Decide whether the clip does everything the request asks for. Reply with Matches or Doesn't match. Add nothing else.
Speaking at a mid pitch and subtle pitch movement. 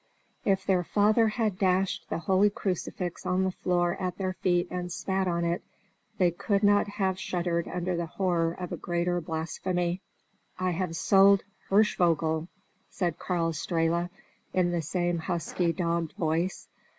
Matches